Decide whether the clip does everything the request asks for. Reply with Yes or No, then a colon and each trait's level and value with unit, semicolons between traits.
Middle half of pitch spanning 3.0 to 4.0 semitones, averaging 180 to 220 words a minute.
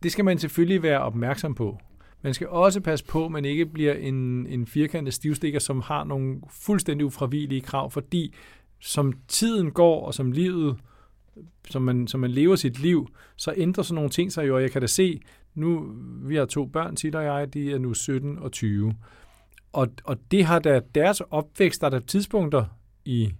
No: average, 4.5 semitones; average, 200 wpm